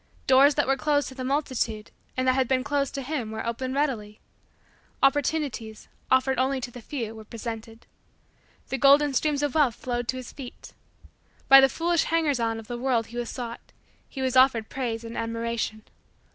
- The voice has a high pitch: Yes, very high, 255 Hz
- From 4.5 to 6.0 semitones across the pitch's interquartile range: No, average, 3.1 semitones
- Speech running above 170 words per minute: Yes, average, 185 wpm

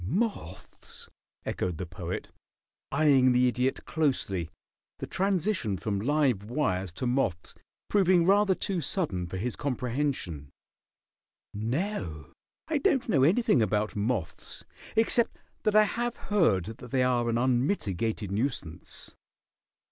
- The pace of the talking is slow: Yes, slow, 120 wpm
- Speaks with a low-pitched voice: Yes, low, 125 Hz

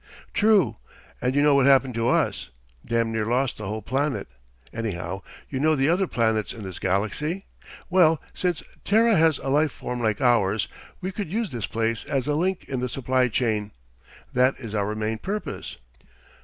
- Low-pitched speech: Yes, low, 125 Hz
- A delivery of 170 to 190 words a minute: Yes, average, 180 wpm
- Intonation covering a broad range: Yes, wide, 5.9 semitones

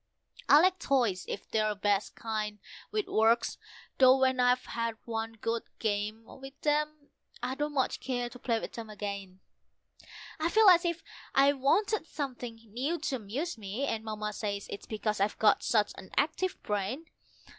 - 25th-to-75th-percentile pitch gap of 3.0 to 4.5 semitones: No, average, 5.1 semitones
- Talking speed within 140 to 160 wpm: No, average, 170 wpm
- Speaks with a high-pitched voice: Yes, high, 235 Hz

